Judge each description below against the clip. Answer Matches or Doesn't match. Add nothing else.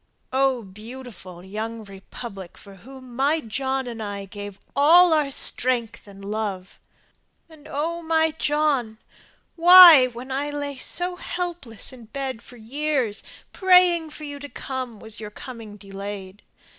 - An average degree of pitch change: Doesn't match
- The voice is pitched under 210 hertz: Doesn't match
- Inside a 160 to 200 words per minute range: Doesn't match